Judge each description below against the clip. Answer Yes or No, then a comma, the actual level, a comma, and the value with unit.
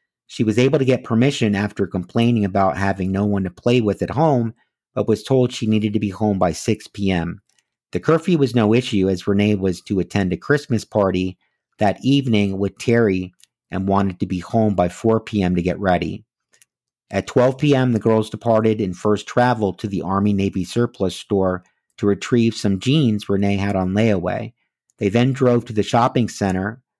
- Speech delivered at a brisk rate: No, average, 190 wpm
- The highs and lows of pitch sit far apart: No, average, 3.5 semitones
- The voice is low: Yes, low, 105 Hz